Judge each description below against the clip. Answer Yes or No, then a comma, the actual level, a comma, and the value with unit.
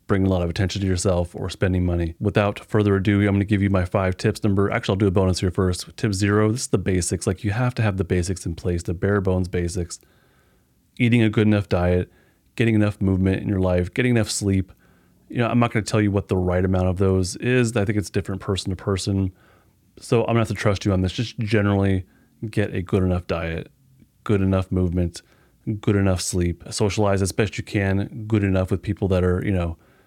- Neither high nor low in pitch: No, low, 100 Hz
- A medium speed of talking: No, fast, 240 wpm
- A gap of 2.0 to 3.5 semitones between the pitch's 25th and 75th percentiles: Yes, narrow, 2.6 semitones